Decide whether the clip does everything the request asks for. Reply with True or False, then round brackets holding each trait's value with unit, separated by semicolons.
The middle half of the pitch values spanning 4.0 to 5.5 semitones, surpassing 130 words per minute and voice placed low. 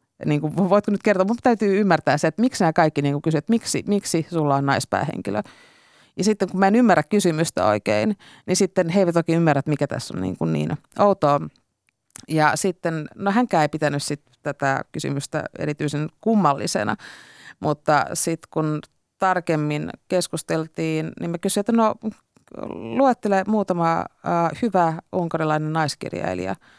False (4.8 semitones; 150 wpm; 165 Hz)